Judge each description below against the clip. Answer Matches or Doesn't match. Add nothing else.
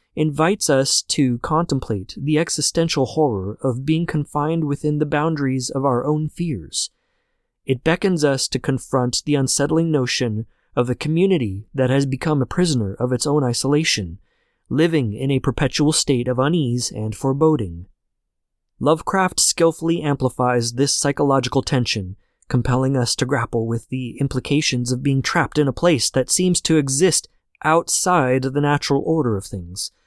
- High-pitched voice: Doesn't match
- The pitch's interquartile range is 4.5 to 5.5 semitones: Doesn't match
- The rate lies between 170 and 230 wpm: Doesn't match